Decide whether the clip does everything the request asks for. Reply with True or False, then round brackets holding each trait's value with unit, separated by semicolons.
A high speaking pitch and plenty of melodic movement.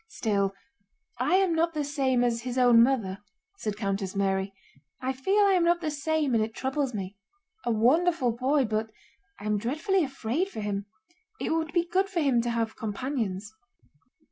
True (255 Hz; 6.5 semitones)